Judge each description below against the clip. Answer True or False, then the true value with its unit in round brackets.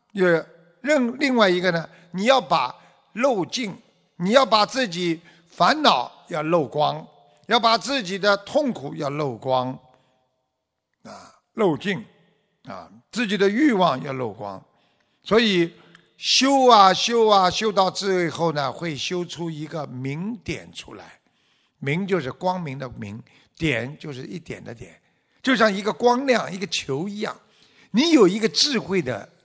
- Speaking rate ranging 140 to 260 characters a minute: True (200 characters per minute)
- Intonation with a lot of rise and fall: True (6.9 semitones)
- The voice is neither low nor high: True (180 Hz)